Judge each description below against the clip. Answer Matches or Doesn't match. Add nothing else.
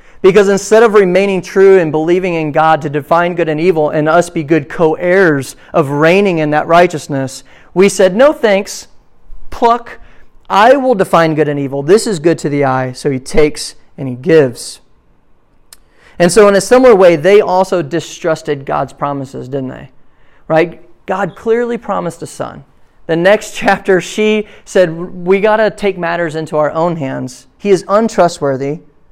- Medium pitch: Matches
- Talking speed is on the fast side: Doesn't match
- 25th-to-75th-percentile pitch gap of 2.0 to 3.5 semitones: Doesn't match